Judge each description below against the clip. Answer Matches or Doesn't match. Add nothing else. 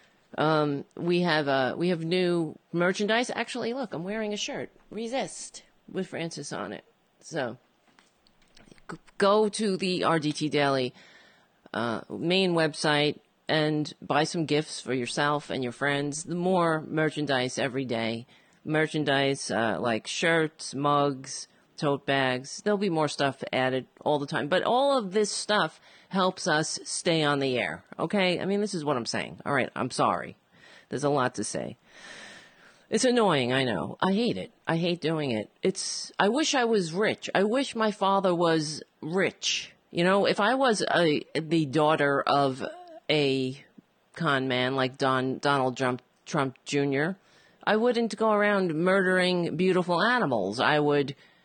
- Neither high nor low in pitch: Matches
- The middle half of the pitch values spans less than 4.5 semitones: Doesn't match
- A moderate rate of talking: Matches